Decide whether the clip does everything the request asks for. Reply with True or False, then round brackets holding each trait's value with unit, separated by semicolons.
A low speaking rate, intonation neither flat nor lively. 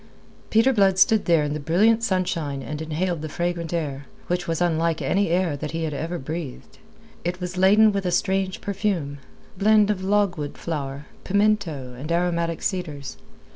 False (170 wpm; 3.9 semitones)